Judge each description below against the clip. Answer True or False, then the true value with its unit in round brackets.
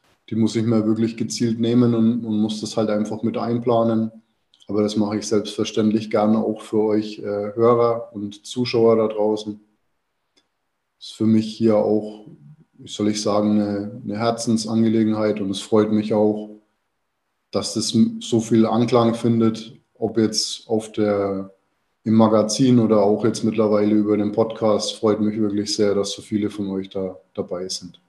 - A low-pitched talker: True (110 Hz)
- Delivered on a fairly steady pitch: True (1.3 semitones)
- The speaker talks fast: False (170 wpm)